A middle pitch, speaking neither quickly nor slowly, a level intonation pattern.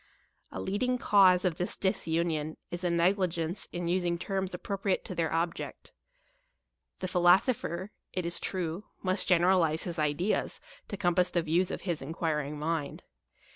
Yes: medium, 175 Hz; average, 150 wpm; narrow, 2.3 semitones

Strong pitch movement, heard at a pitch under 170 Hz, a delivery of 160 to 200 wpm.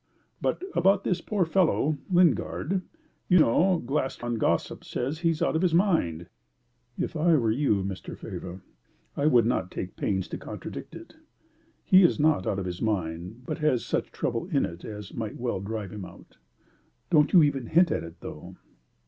Yes: wide, 8.8 semitones; low, 135 Hz; average, 180 wpm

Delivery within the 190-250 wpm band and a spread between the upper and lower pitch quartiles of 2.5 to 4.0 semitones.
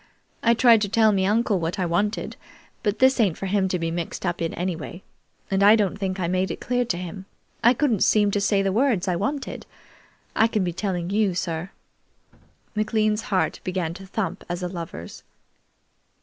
Yes: average, 195 wpm; average, 3.2 semitones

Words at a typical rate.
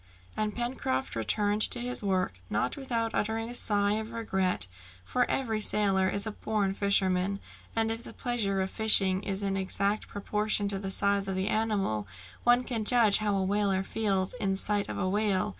Yes: average, 185 wpm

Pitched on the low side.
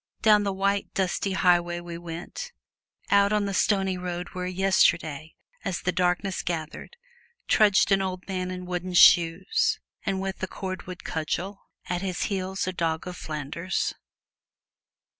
No: medium, 185 Hz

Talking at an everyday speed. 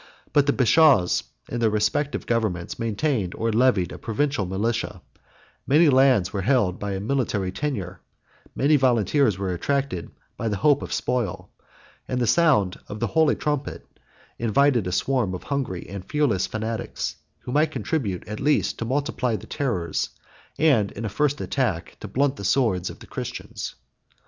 Yes: average, 165 wpm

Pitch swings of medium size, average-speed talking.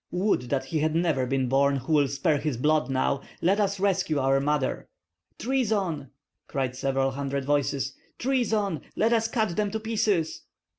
No: wide, 6.8 semitones; average, 165 wpm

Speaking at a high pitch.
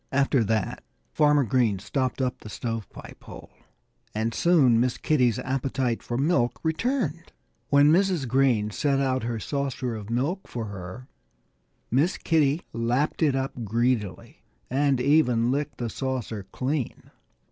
No: low, 130 Hz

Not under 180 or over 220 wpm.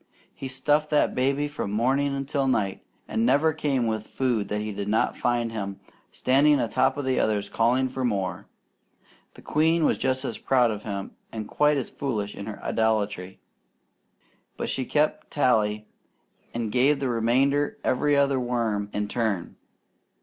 No: average, 165 wpm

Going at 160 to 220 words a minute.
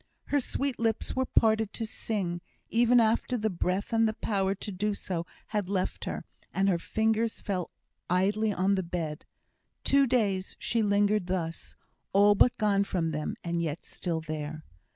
Yes: average, 170 wpm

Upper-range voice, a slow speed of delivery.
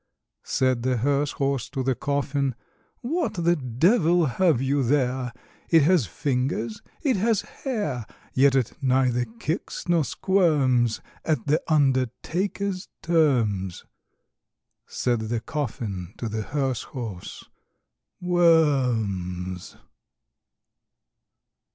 No: low, 135 Hz; slow, 100 wpm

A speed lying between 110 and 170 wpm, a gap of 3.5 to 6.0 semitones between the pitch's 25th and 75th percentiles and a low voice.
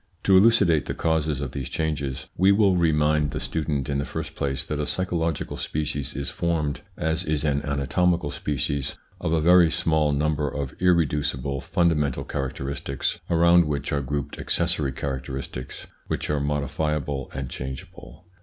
No: average, 155 wpm; average, 2.8 semitones; very low, 75 Hz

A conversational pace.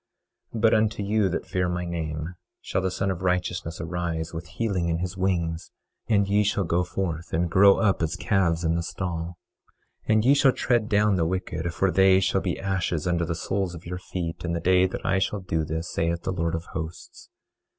No: fast, 215 wpm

